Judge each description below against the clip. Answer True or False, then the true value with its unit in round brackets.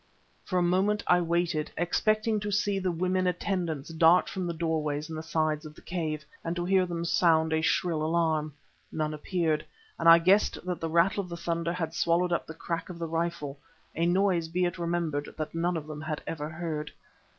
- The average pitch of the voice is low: False (170 Hz)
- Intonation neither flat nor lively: False (2.1 semitones)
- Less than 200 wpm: False (205 wpm)